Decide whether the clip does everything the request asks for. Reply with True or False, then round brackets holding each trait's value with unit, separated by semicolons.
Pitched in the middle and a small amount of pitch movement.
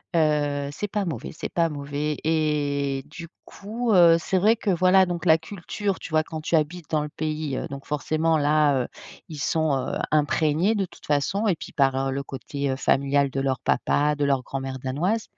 False (150 Hz; 3.3 semitones)